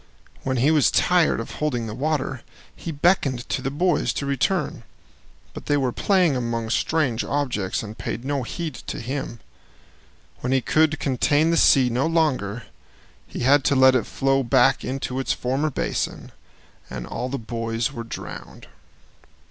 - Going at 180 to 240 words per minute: No, average, 165 wpm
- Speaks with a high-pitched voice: No, low, 135 Hz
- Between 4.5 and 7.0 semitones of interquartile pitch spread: No, average, 3.6 semitones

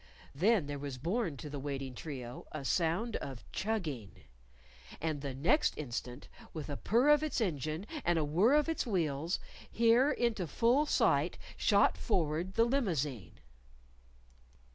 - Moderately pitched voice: Yes, medium, 165 Hz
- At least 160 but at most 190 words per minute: No, average, 145 wpm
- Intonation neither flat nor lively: No, wide, 8.3 semitones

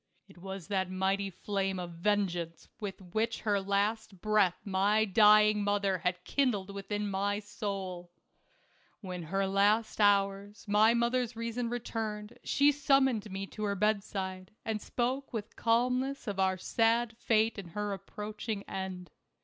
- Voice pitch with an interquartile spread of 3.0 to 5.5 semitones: No, narrow, 2.5 semitones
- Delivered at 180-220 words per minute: No, average, 145 wpm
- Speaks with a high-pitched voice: Yes, high, 205 Hz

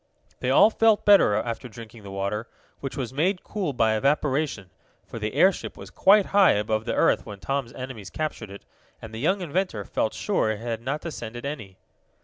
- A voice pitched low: Yes, low, 120 Hz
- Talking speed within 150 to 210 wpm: Yes, average, 190 wpm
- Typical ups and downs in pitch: No, wide, 6.2 semitones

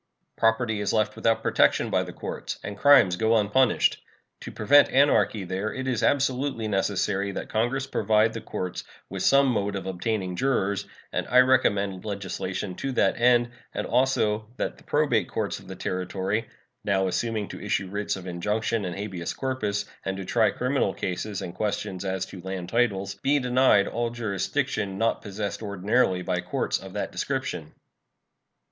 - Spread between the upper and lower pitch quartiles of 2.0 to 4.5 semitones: Yes, average, 3.8 semitones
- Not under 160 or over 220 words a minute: Yes, average, 165 wpm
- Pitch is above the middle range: No, low, 105 Hz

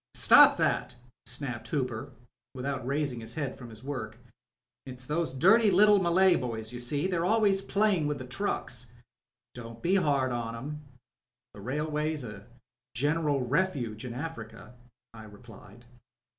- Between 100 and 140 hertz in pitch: Yes, low, 135 Hz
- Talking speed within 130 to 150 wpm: Yes, average, 145 wpm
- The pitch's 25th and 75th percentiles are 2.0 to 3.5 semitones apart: No, average, 5.3 semitones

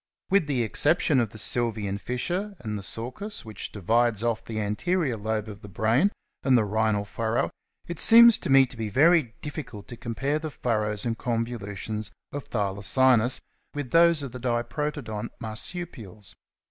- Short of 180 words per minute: Yes, average, 160 wpm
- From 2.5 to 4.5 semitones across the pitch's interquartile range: No, average, 4.9 semitones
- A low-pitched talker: Yes, low, 120 Hz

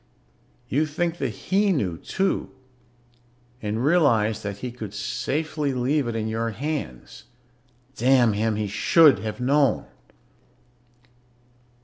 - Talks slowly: Yes, slow, 115 wpm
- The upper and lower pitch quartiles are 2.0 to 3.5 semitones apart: No, wide, 5.6 semitones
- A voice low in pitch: Yes, low, 125 Hz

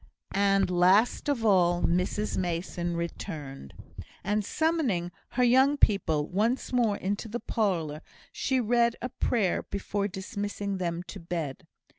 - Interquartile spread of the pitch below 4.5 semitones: No, average, 4.8 semitones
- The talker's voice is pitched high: Yes, high, 200 Hz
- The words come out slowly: Yes, slow, 130 wpm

